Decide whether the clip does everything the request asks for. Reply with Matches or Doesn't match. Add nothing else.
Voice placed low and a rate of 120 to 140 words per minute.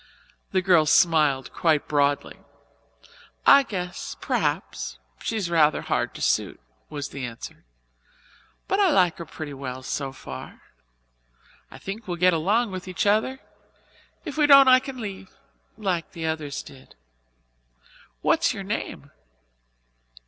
Doesn't match